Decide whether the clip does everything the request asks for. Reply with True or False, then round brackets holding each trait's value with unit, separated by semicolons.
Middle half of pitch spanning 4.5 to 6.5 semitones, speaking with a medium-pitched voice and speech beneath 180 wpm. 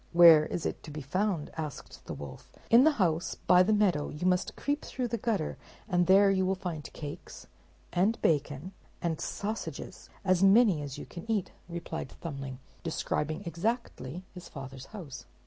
True (4.9 semitones; 175 Hz; 170 wpm)